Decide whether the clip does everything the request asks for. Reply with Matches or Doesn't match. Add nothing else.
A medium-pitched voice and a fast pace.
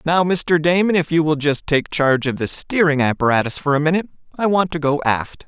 Matches